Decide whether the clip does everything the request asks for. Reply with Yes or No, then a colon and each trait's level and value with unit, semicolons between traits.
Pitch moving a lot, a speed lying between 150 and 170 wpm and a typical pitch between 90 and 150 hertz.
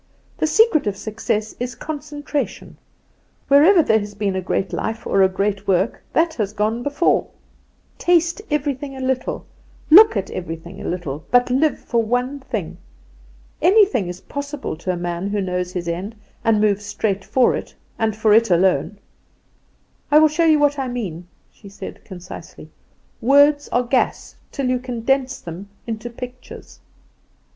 No: wide, 6.4 semitones; average, 160 wpm; high, 230 Hz